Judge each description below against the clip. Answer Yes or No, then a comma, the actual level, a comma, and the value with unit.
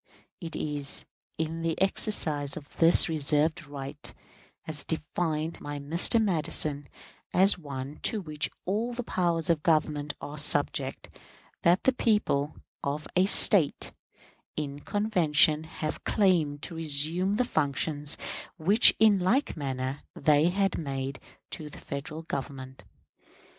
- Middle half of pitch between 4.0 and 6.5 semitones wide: No, average, 3.6 semitones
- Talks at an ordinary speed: No, slow, 125 wpm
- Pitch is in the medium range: Yes, medium, 155 Hz